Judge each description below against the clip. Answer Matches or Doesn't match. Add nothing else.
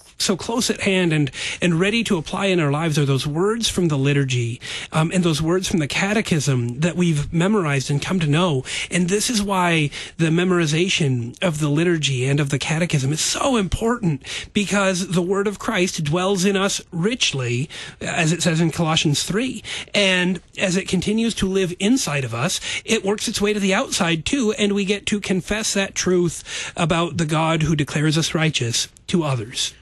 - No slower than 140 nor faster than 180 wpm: Doesn't match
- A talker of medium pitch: Matches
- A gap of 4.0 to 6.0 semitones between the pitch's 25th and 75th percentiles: Matches